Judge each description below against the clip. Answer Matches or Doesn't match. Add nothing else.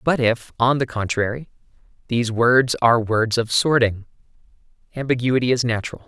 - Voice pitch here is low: Matches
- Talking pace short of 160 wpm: Matches